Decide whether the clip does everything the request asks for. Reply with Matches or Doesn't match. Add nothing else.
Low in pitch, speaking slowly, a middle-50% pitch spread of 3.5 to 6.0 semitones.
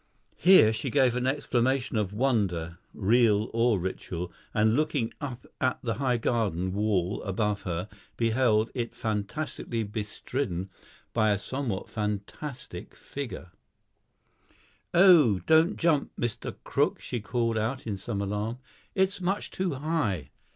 Matches